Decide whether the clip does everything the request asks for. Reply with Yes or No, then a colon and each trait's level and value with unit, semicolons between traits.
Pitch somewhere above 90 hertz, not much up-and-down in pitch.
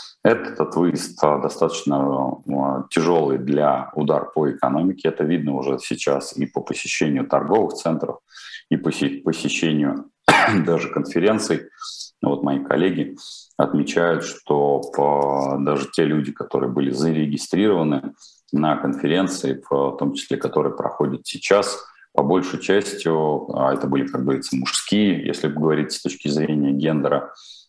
No: very low, 70 Hz; narrow, 1.8 semitones